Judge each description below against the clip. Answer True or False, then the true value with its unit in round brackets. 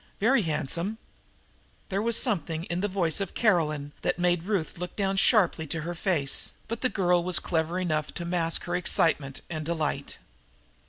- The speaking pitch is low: False (175 Hz)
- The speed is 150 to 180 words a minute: True (170 wpm)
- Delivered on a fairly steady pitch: False (3.2 semitones)